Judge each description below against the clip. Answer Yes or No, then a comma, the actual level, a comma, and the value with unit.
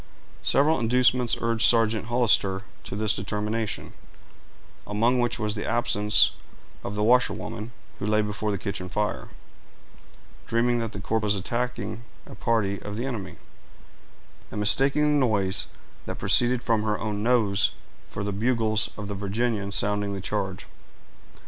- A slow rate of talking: No, average, 145 wpm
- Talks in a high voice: No, low, 110 Hz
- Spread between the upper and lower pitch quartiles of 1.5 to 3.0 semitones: Yes, narrow, 2.6 semitones